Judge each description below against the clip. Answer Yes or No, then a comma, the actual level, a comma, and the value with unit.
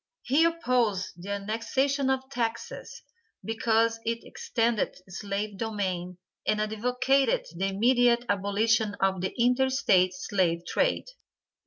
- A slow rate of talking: Yes, slow, 115 wpm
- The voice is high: Yes, high, 225 Hz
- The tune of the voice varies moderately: Yes, average, 3.9 semitones